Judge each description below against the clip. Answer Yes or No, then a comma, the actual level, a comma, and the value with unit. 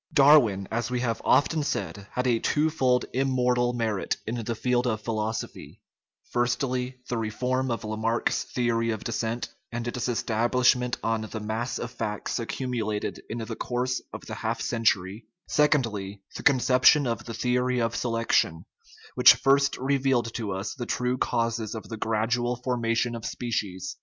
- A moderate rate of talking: Yes, average, 160 wpm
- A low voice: Yes, low, 120 Hz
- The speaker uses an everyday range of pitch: No, narrow, 2.2 semitones